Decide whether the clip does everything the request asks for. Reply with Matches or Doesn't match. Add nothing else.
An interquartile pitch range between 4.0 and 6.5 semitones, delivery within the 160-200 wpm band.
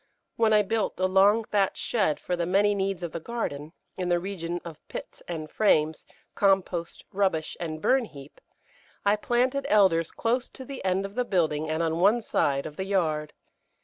Matches